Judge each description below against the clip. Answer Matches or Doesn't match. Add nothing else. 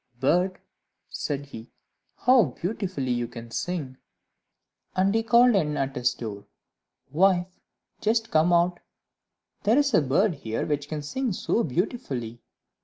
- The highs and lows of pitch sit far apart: Matches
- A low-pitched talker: Doesn't match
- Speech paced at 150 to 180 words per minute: Doesn't match